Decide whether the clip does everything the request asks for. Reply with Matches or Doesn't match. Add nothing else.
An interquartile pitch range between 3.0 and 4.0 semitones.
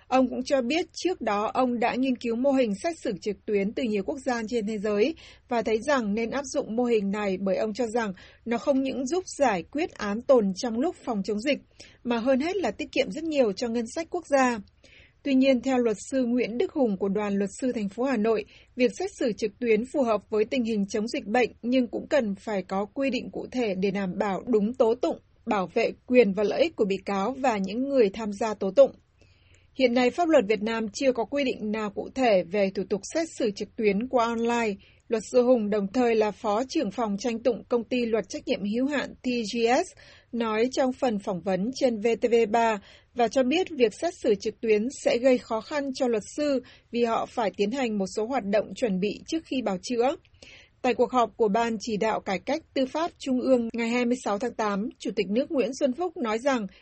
Matches